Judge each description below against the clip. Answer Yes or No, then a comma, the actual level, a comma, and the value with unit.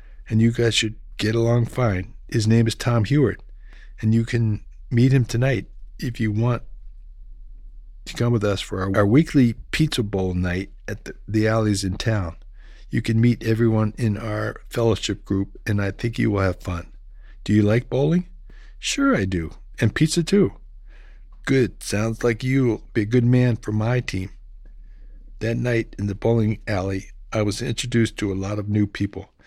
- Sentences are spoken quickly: No, average, 180 wpm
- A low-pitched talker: Yes, low, 110 Hz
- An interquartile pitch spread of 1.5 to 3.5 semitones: Yes, average, 3.1 semitones